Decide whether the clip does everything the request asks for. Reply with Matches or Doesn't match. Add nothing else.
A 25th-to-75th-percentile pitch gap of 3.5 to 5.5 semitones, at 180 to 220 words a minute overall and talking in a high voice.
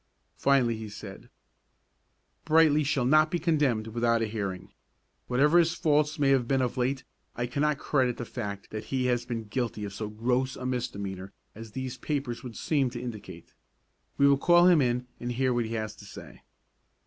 Doesn't match